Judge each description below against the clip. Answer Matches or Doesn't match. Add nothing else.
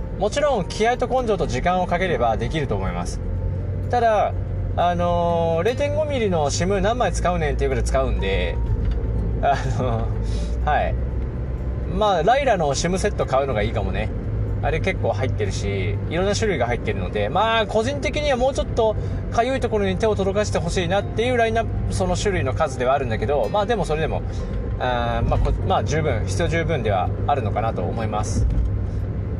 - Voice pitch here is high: Doesn't match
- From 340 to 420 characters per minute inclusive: Matches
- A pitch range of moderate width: Matches